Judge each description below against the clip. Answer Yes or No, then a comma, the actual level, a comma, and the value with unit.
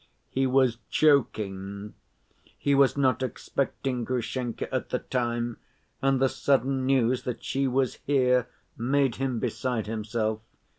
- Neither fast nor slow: No, slow, 130 wpm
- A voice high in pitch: No, low, 125 Hz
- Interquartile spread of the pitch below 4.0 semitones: Yes, narrow, 2.6 semitones